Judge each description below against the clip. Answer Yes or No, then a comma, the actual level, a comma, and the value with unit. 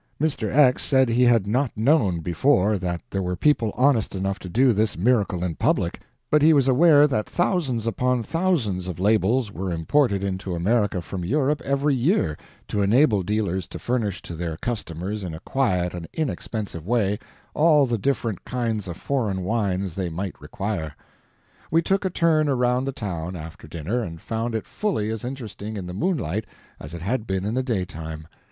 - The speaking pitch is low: Yes, low, 110 Hz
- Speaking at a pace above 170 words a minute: Yes, average, 185 wpm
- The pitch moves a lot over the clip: Yes, wide, 6.1 semitones